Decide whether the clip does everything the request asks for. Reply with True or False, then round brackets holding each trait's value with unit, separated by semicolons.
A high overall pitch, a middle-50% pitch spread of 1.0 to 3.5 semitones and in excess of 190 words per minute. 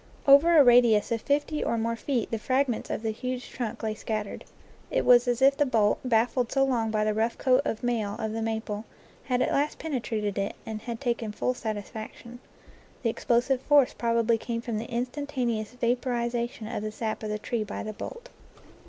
True (235 Hz; 2.5 semitones; 200 wpm)